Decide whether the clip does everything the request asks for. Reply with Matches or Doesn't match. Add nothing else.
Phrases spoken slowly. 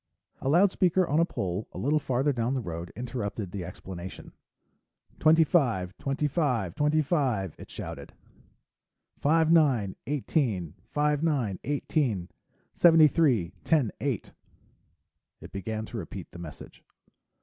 Matches